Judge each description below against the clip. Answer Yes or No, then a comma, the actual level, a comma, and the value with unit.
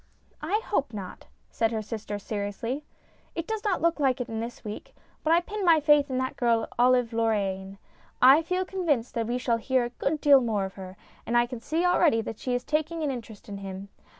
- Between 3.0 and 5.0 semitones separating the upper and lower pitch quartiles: No, wide, 5.6 semitones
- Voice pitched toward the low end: No, high, 245 Hz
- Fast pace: Yes, fast, 220 wpm